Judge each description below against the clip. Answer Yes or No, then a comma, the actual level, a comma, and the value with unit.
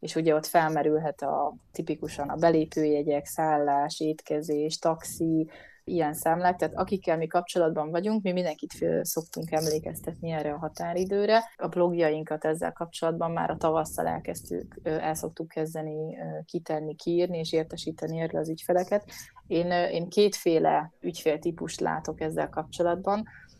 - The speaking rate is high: No, average, 125 wpm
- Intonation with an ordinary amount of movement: No, narrow, 2.0 semitones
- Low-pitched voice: No, medium, 160 Hz